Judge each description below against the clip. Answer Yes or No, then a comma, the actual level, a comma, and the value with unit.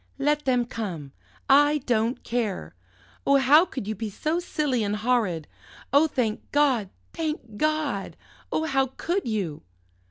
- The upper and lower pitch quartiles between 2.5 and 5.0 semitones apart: No, wide, 5.5 semitones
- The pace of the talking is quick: No, average, 140 wpm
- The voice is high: Yes, very high, 250 Hz